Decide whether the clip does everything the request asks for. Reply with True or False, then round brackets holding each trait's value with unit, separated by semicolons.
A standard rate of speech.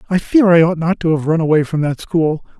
False (275 wpm)